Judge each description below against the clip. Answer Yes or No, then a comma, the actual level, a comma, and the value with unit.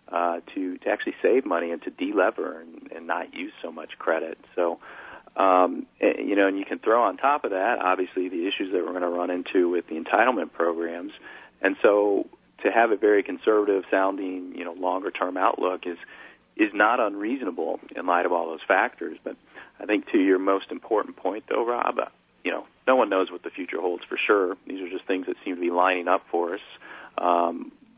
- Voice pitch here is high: No, very low, 95 Hz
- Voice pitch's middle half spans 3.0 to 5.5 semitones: No, narrow, 2.4 semitones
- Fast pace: Yes, fast, 215 wpm